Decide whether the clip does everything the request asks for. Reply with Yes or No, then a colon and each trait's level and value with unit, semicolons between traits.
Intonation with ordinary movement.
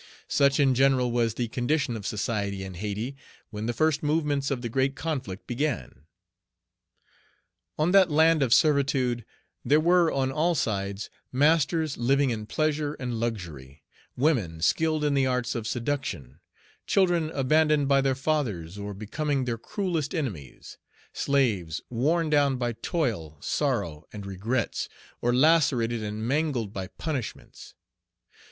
No: wide, 5.7 semitones